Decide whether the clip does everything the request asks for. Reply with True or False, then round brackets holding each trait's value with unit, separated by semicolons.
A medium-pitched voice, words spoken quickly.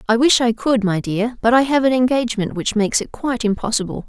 False (235 Hz; 235 wpm)